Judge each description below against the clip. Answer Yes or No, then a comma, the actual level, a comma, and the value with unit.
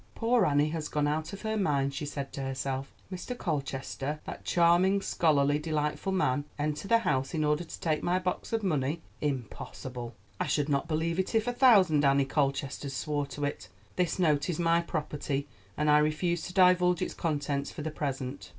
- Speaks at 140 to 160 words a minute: No, average, 185 wpm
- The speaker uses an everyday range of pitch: Yes, average, 3.8 semitones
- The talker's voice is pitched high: No, medium, 150 Hz